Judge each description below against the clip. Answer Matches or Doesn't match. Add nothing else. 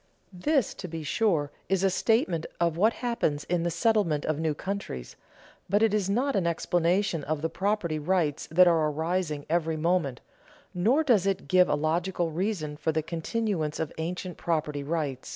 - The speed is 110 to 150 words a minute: Doesn't match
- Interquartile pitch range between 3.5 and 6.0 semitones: Matches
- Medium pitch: Matches